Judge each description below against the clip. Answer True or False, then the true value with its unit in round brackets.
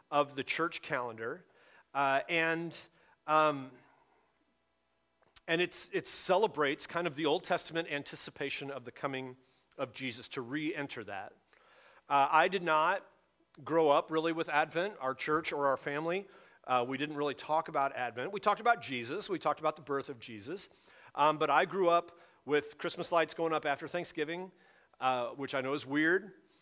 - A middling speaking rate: True (170 wpm)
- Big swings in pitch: False (3.3 semitones)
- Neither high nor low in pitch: True (150 Hz)